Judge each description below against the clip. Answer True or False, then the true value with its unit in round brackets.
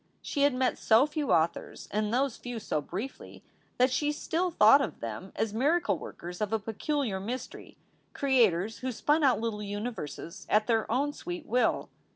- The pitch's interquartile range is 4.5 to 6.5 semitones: True (5.1 semitones)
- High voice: True (235 Hz)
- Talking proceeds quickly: False (175 wpm)